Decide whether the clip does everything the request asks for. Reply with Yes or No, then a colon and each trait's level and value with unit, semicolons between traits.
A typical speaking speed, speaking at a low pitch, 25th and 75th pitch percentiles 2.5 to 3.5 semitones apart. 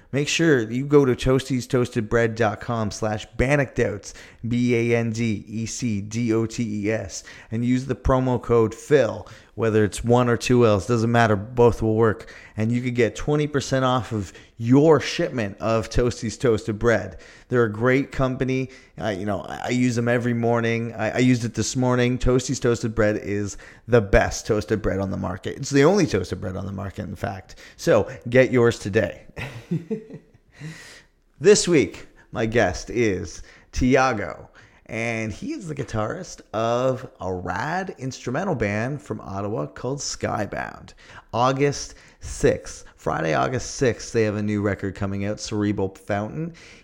Yes: average, 165 wpm; low, 115 Hz; average, 3.1 semitones